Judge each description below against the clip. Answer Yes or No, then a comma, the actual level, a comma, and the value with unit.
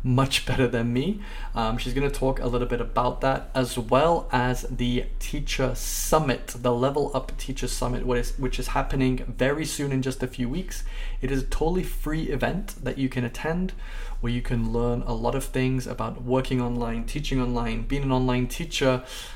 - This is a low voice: Yes, low, 130 Hz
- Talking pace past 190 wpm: Yes, average, 200 wpm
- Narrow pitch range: Yes, narrow, 1.5 semitones